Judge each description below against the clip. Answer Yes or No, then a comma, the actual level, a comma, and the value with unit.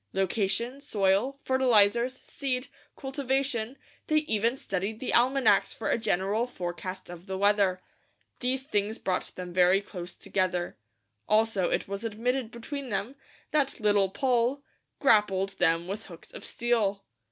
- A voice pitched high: Yes, high, 215 Hz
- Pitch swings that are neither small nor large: Yes, average, 4.8 semitones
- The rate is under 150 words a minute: Yes, slow, 135 wpm